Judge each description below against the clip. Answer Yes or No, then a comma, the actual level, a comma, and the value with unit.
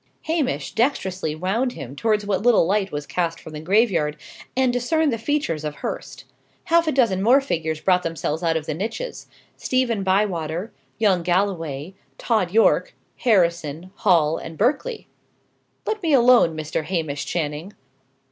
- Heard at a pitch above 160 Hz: Yes, high, 190 Hz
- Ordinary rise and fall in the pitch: No, wide, 6.8 semitones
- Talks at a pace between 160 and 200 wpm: No, average, 150 wpm